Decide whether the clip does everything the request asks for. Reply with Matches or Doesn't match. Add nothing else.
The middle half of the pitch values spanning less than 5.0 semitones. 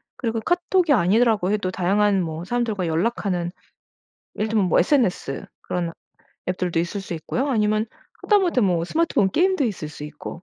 Doesn't match